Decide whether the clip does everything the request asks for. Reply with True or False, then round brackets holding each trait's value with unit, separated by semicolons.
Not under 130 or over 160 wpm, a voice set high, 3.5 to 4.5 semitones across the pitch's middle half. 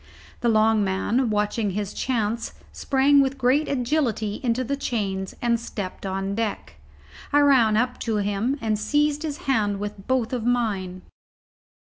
True (145 wpm; 230 Hz; 4.0 semitones)